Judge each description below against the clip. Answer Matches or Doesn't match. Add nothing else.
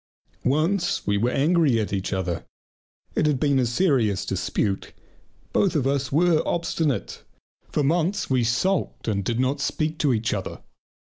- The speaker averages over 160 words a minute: Doesn't match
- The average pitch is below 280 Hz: Matches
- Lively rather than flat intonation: Matches